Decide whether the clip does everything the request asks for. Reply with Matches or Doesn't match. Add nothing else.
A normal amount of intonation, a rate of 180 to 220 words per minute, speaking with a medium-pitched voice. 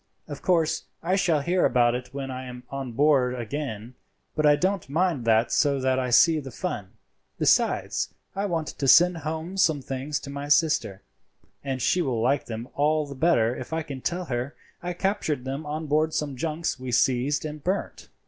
Matches